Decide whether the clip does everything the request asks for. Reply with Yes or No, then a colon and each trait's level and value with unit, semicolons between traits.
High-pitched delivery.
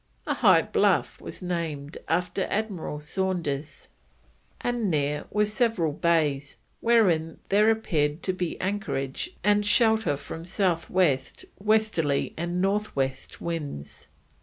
No: medium, 175 Hz